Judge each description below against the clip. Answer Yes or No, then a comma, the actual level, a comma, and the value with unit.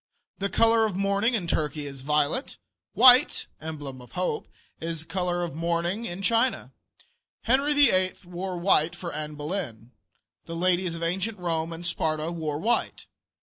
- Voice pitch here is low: No, medium, 175 Hz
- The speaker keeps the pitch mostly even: No, average, 4.0 semitones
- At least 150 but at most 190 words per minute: Yes, average, 155 wpm